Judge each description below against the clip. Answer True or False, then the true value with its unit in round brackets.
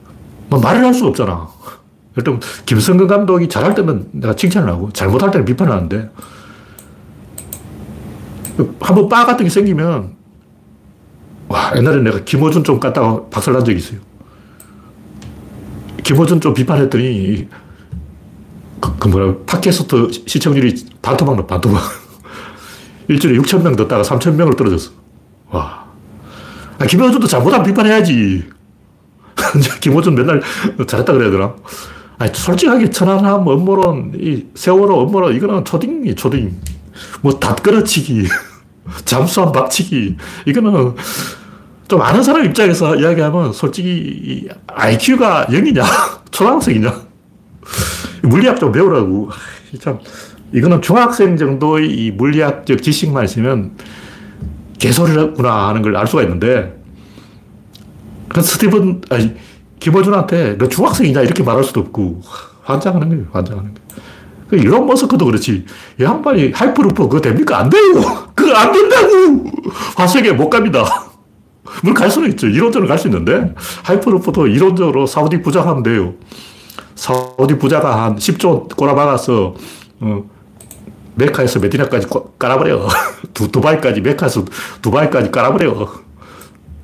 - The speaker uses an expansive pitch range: True (8.8 semitones)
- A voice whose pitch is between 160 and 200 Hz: False (135 Hz)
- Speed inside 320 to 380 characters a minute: False (290 characters per minute)